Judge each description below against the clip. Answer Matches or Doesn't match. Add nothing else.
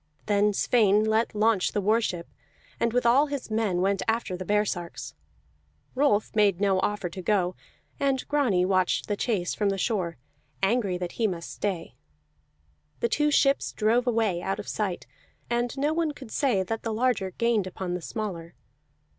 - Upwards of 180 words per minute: Doesn't match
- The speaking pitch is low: Doesn't match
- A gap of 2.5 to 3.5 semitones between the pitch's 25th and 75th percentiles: Doesn't match